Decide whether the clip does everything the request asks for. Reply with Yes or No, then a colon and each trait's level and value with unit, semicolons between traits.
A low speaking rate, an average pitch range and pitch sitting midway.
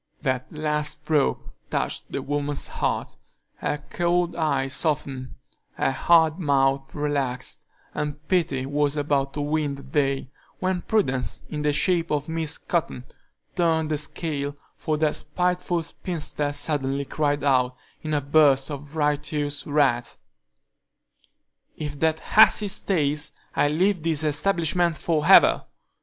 No: slow, 130 wpm; narrow, 2.3 semitones; medium, 150 Hz